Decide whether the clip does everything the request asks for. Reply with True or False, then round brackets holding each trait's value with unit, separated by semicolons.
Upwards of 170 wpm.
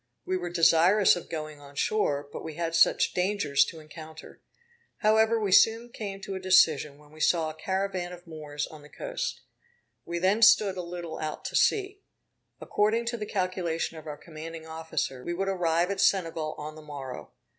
True (190 wpm)